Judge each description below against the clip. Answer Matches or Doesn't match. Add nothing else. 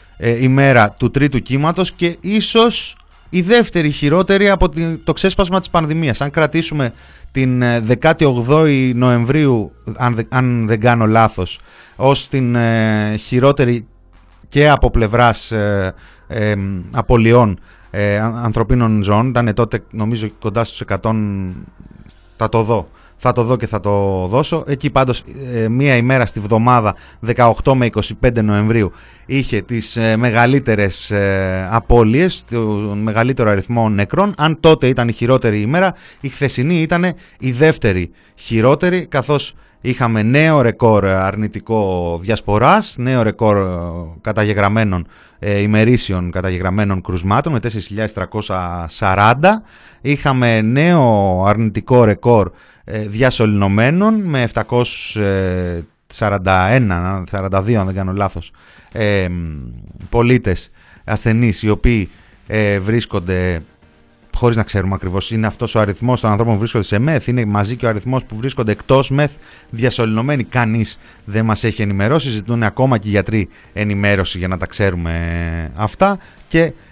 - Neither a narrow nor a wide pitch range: Matches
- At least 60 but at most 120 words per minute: Matches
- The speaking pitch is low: Matches